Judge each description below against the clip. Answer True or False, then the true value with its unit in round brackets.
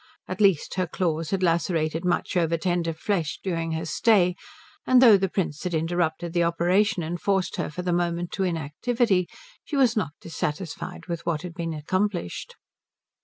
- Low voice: False (175 Hz)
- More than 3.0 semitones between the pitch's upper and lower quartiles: False (2.5 semitones)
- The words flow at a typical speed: True (170 wpm)